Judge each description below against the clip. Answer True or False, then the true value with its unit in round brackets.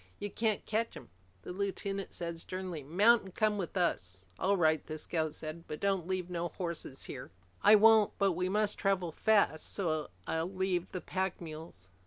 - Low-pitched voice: False (180 Hz)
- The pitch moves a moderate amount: True (3.5 semitones)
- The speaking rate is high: False (185 wpm)